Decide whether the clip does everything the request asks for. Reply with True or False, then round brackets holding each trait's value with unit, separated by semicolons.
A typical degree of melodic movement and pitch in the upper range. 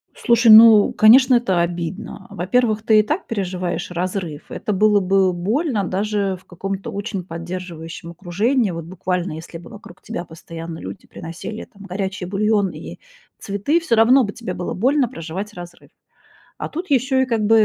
True (4.1 semitones; 195 Hz)